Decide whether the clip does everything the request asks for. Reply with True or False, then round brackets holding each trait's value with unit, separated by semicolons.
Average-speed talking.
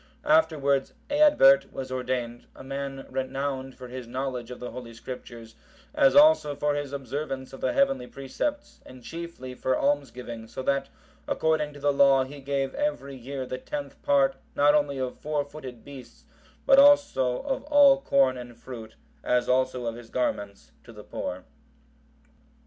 True (160 wpm)